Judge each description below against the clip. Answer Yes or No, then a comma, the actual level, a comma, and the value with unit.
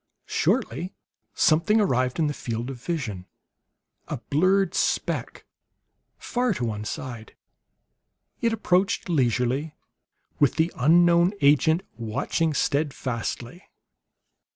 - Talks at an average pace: No, slow, 100 wpm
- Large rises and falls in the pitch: Yes, wide, 6.0 semitones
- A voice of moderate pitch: Yes, medium, 150 Hz